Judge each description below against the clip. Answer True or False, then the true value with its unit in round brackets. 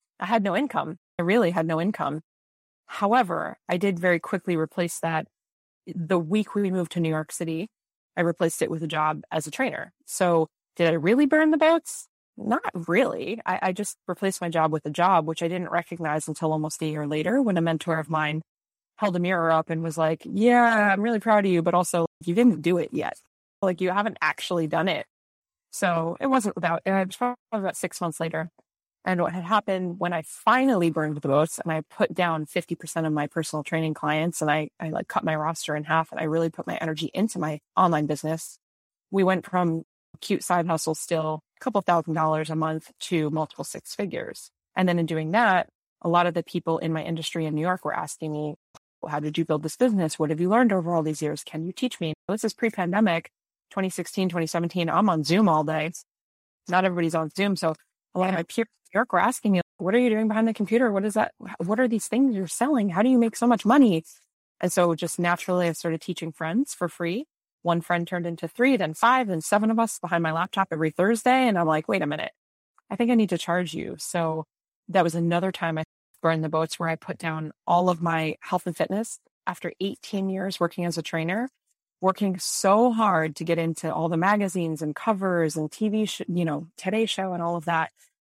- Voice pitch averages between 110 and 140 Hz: False (175 Hz)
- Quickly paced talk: True (225 wpm)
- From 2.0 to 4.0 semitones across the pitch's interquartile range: True (3.7 semitones)